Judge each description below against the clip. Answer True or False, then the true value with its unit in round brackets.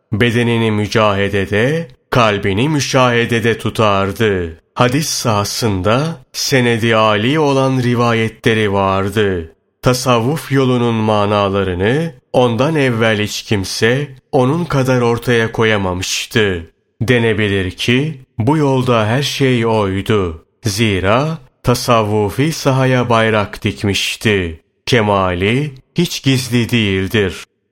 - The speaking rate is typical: False (85 wpm)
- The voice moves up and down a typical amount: True (3.9 semitones)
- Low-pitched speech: True (115 Hz)